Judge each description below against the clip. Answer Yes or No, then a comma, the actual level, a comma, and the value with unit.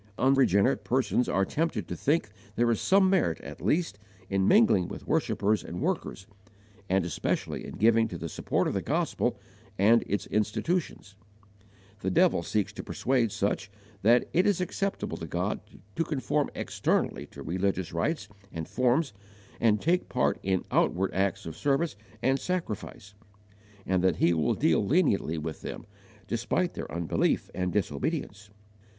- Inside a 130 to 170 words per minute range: Yes, average, 155 wpm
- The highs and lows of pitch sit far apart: Yes, wide, 6.7 semitones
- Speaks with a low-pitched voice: Yes, low, 105 Hz